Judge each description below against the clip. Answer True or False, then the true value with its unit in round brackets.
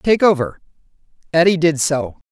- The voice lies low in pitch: False (170 Hz)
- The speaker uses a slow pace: True (130 wpm)